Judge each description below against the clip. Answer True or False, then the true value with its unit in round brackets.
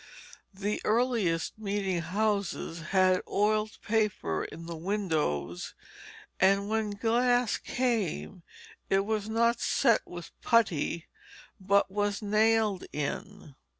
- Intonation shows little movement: False (3.3 semitones)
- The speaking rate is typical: False (105 wpm)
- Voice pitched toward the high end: True (205 Hz)